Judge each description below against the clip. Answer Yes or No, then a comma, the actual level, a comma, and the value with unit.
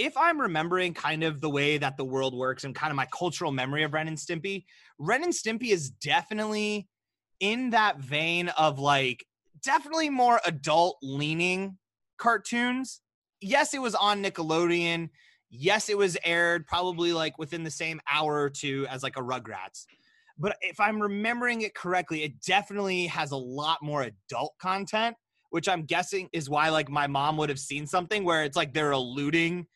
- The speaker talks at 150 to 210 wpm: Yes, average, 175 wpm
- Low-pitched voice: No, medium, 170 Hz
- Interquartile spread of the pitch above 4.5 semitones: Yes, average, 5.2 semitones